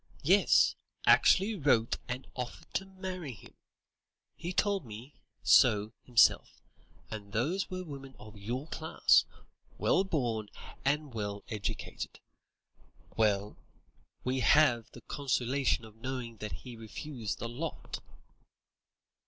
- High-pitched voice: No, low, 125 Hz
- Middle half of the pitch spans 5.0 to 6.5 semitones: Yes, wide, 5.5 semitones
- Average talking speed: No, slow, 115 wpm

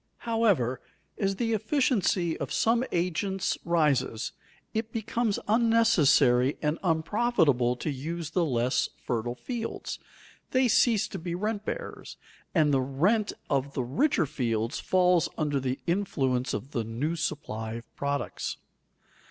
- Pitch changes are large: Yes, wide, 8.3 semitones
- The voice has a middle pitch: Yes, medium, 165 Hz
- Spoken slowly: Yes, slow, 130 wpm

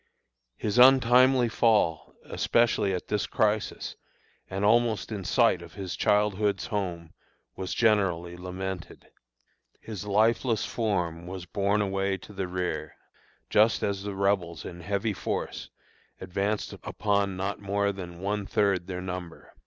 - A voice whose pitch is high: No, low, 100 Hz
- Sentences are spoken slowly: Yes, slow, 130 wpm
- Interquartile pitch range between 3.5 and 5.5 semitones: No, narrow, 2.5 semitones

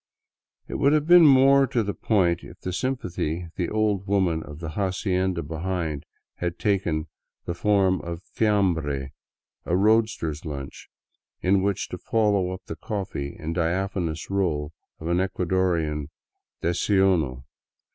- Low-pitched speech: Yes, very low, 90 Hz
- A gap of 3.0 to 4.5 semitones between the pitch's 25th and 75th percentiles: Yes, average, 3.7 semitones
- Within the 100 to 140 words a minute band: Yes, slow, 135 wpm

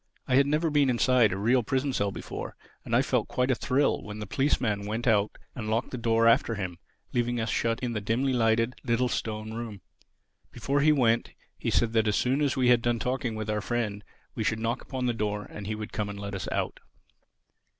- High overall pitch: No, low, 115 Hz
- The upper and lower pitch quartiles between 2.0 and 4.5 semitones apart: Yes, average, 3.0 semitones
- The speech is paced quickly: Yes, fast, 225 wpm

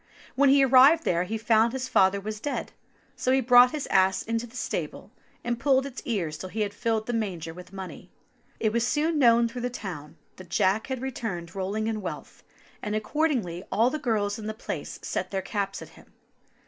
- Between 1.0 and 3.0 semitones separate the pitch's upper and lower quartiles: No, average, 4.5 semitones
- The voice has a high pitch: Yes, high, 220 Hz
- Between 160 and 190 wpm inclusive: No, fast, 205 wpm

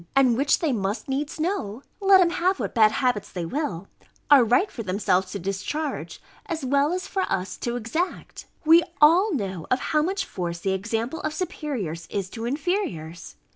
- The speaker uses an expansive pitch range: Yes, wide, 8.4 semitones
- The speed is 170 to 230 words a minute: Yes, average, 180 wpm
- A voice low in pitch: No, very high, 255 Hz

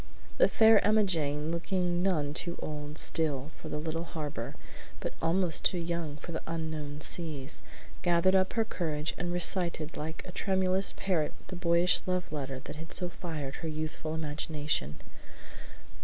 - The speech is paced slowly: No, average, 155 wpm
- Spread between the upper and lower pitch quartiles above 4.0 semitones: No, average, 3.0 semitones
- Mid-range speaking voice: Yes, medium, 165 Hz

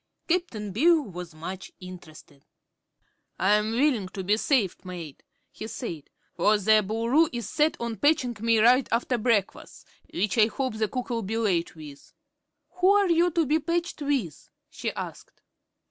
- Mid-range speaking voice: No, high, 225 Hz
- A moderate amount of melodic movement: No, wide, 6.8 semitones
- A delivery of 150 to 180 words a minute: Yes, average, 160 wpm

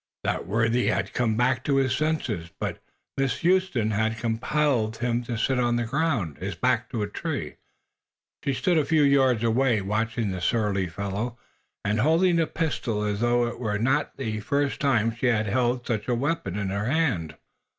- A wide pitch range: No, average, 4.2 semitones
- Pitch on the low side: Yes, low, 120 Hz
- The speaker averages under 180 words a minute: No, average, 185 wpm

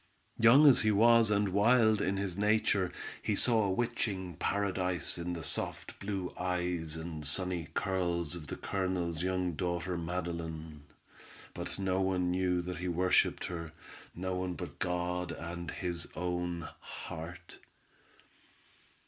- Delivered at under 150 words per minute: Yes, average, 140 wpm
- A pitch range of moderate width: No, narrow, 2.1 semitones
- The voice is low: Yes, very low, 90 Hz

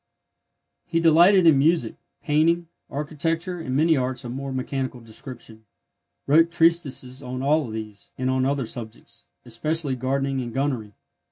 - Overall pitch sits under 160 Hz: Yes, low, 135 Hz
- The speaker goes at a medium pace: Yes, average, 145 wpm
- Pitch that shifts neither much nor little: Yes, average, 4.3 semitones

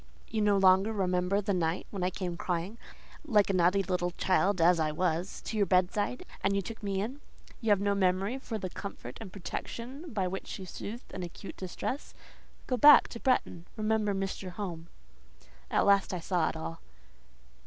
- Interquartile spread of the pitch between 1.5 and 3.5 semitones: Yes, average, 2.8 semitones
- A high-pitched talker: Yes, high, 195 Hz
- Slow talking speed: No, average, 185 wpm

